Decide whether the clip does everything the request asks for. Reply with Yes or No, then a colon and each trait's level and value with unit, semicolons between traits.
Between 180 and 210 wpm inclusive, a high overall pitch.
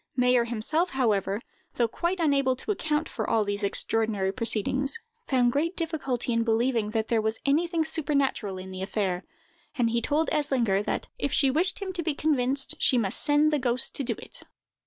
Yes: average, 185 wpm; very high, 255 Hz